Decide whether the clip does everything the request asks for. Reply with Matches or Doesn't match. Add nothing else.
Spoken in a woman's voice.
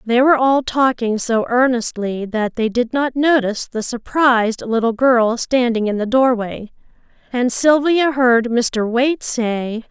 Matches